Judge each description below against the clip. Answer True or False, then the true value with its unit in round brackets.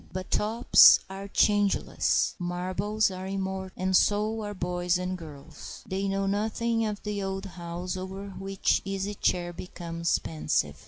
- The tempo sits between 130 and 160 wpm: True (150 wpm)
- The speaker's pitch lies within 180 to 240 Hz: True (190 Hz)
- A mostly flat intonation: True (2.2 semitones)